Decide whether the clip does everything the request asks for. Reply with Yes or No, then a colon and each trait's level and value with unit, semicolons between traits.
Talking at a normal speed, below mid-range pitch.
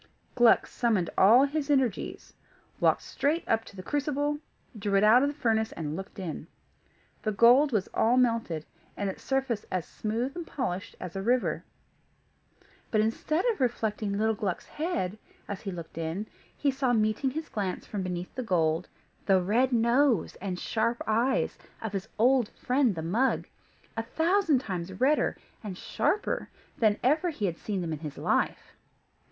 No: average, 170 wpm; high, 220 Hz